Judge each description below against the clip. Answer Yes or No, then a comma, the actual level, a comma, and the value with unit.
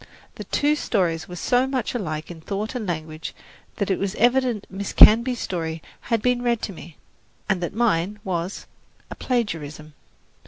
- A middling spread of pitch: No, wide, 6.3 semitones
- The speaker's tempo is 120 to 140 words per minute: No, average, 165 wpm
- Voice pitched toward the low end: No, high, 200 Hz